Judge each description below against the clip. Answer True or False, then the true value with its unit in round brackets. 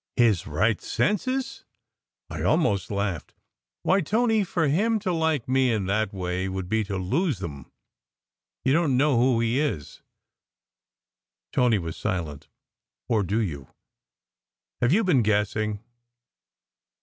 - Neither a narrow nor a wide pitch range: False (8.2 semitones)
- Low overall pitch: True (115 Hz)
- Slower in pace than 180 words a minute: True (135 wpm)